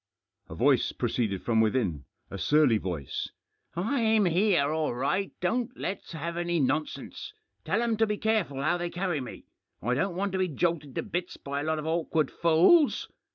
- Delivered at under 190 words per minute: No, average, 195 wpm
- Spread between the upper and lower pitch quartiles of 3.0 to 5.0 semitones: No, wide, 5.5 semitones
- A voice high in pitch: No, medium, 165 Hz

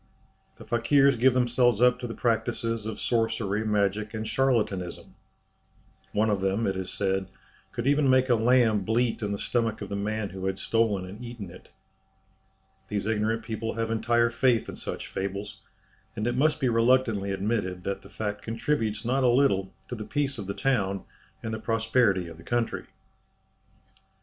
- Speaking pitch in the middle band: No, low, 110 Hz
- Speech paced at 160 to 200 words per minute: Yes, average, 175 wpm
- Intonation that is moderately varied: Yes, average, 3.2 semitones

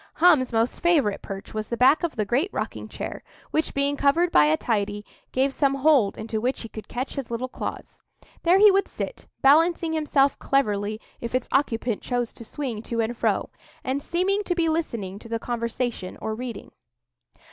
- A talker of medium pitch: No, very high, 255 Hz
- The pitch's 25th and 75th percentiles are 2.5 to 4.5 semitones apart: No, average, 5.2 semitones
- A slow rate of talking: No, average, 190 wpm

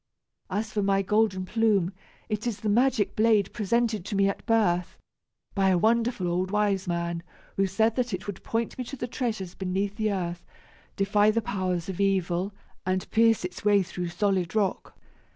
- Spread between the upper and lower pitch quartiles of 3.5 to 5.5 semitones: No, average, 3.0 semitones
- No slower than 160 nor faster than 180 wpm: Yes, average, 175 wpm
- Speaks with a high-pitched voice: Yes, high, 200 Hz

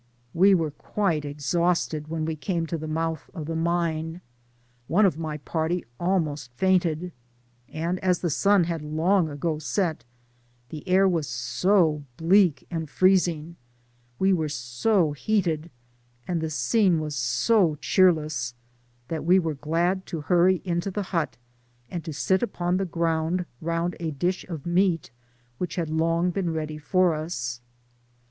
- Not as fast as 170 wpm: Yes, average, 155 wpm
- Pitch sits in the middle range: Yes, medium, 165 Hz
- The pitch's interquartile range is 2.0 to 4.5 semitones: Yes, average, 2.8 semitones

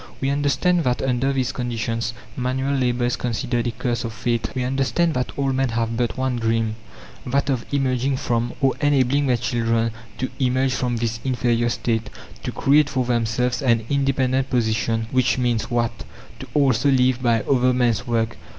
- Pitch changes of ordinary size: No, narrow, 2.2 semitones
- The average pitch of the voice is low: Yes, low, 125 Hz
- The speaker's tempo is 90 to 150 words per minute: No, average, 175 wpm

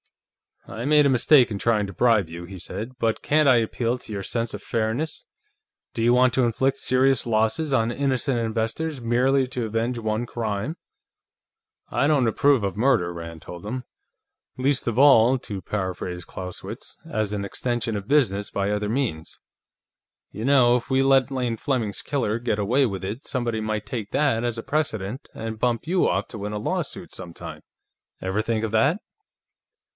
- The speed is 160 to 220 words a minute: Yes, average, 180 wpm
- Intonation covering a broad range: No, average, 3.9 semitones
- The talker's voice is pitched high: No, low, 115 Hz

